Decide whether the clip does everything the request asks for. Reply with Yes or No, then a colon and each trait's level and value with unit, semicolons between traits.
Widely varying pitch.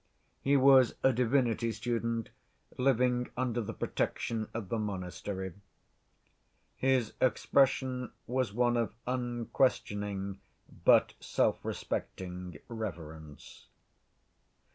No: average, 3.9 semitones